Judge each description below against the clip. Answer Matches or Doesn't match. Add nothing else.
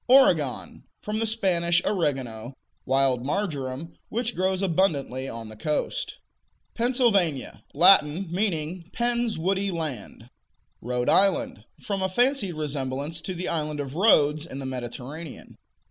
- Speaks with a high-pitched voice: Doesn't match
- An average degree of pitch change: Doesn't match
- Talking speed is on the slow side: Matches